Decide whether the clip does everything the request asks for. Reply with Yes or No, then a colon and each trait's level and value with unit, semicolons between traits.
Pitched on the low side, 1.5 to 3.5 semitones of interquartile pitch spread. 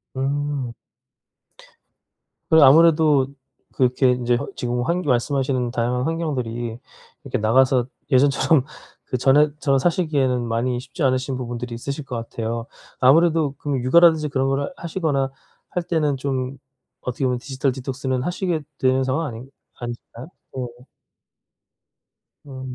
Yes: low, 130 Hz; average, 2.7 semitones